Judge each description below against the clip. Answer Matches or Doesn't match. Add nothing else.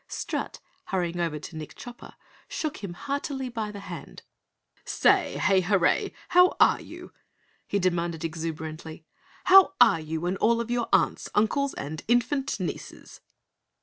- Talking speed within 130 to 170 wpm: Matches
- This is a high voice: Matches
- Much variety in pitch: Matches